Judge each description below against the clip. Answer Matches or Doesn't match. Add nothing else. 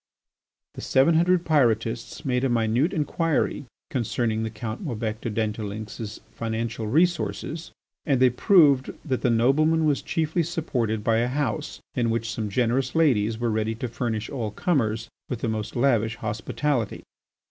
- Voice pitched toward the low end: Matches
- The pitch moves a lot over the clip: Doesn't match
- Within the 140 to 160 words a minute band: Matches